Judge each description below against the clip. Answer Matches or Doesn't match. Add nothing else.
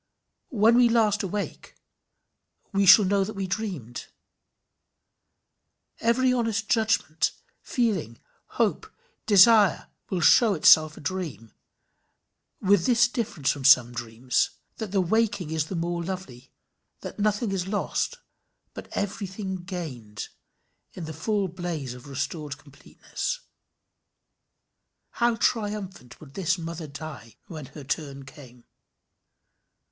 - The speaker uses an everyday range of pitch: Doesn't match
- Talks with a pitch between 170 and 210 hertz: Matches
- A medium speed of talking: Doesn't match